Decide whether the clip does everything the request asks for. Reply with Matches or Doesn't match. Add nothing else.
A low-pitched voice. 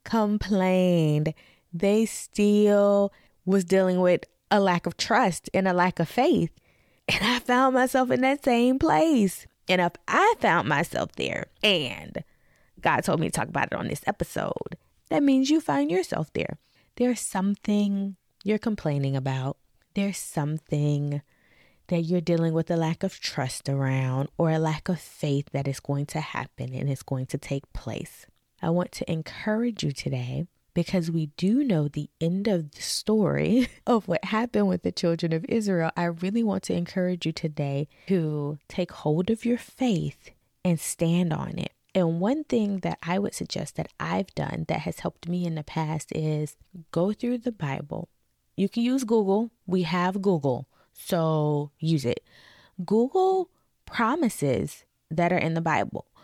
Doesn't match